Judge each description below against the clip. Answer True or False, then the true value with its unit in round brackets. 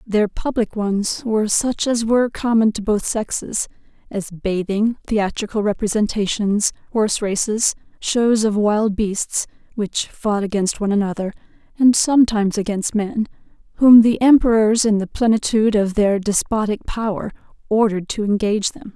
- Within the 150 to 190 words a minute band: False (140 wpm)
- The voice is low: False (215 Hz)